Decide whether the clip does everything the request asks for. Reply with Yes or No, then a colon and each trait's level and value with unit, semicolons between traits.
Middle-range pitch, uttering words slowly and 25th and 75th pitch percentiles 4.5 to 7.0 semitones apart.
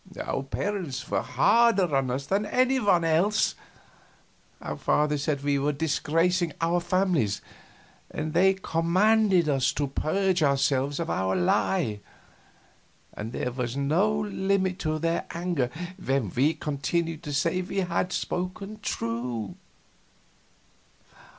Yes: medium, 165 Hz; slow, 125 wpm; average, 5.3 semitones